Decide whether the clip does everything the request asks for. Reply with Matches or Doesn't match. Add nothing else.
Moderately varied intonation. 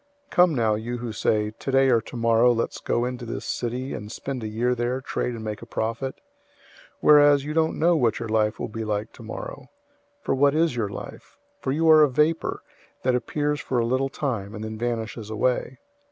Matches